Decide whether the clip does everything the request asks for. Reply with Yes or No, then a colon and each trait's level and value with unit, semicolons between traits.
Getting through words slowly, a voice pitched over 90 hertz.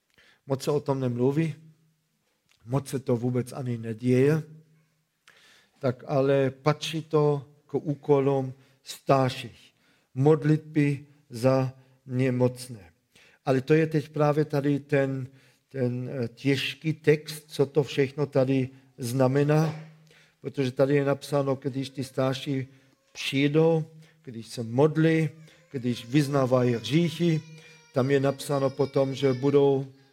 Yes: slow, 110 wpm; medium, 140 Hz